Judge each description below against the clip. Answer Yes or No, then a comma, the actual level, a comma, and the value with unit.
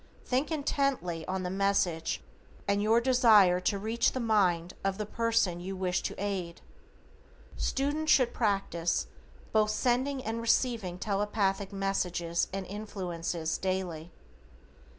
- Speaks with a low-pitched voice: No, high, 200 Hz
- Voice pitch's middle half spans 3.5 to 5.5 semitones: Yes, average, 4.2 semitones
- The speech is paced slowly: Yes, slow, 125 wpm